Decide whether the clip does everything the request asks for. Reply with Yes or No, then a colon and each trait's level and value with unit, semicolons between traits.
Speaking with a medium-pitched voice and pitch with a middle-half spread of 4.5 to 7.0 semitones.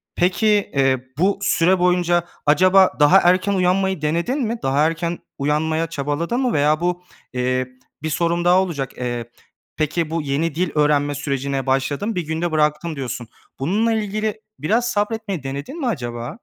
Yes: medium, 165 Hz; average, 4.8 semitones